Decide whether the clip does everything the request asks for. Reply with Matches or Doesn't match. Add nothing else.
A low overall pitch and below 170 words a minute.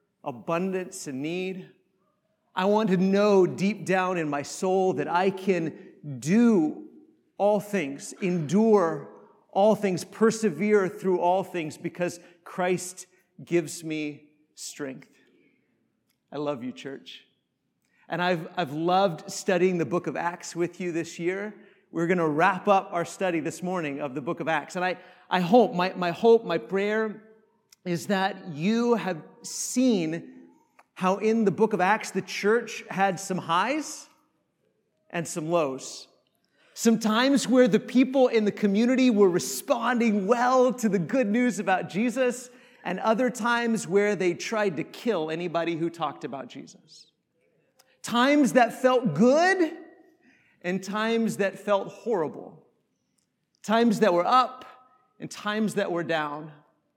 Doesn't match